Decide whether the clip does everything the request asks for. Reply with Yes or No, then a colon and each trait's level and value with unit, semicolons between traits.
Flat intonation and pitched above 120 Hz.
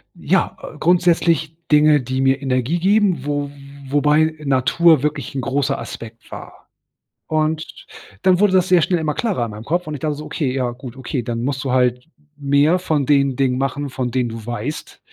No: average, 3.5 semitones; medium, 140 Hz